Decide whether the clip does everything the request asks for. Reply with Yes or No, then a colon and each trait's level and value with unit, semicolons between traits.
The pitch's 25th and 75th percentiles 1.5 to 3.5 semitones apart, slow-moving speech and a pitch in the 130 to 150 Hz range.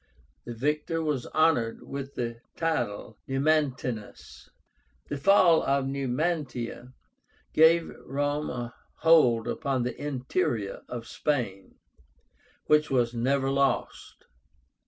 No: average, 3.9 semitones; slow, 105 wpm; low, 135 Hz